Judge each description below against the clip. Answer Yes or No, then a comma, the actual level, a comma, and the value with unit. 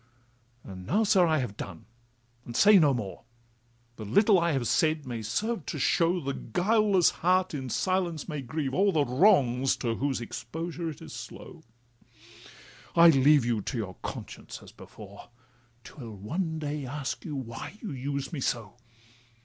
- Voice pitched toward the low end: No, medium, 145 Hz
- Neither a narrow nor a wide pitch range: No, wide, 6.3 semitones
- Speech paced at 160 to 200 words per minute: Yes, average, 165 wpm